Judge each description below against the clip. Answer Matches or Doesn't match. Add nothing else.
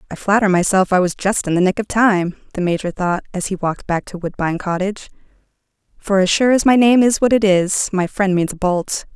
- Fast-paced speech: Matches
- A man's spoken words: Doesn't match